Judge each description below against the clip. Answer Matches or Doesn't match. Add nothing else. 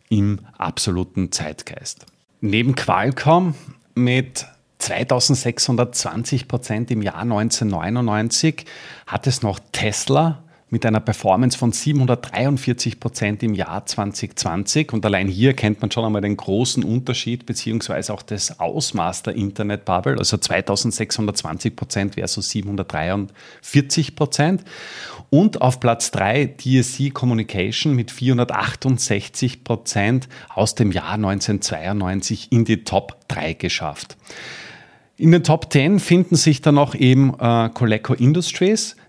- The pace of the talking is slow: Matches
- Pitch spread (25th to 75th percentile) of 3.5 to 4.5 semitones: Matches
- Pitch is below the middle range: Matches